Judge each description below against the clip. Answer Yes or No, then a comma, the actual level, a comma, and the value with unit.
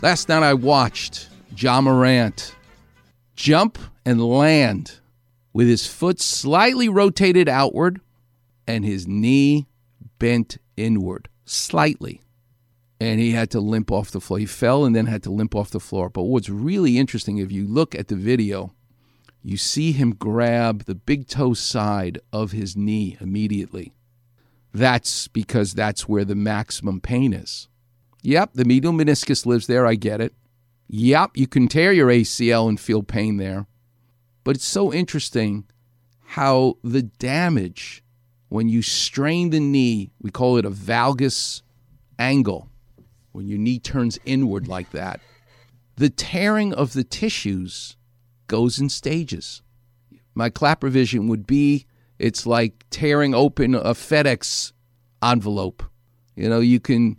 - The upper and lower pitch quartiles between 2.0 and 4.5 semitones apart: Yes, average, 3.5 semitones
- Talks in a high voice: No, low, 120 Hz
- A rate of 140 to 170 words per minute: Yes, average, 145 wpm